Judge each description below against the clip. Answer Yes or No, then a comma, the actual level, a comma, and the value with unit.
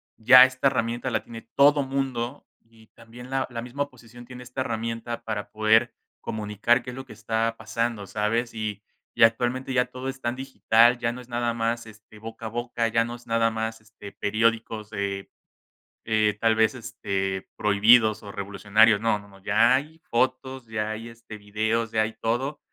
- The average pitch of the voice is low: Yes, low, 115 Hz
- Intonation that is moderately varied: No, narrow, 2.0 semitones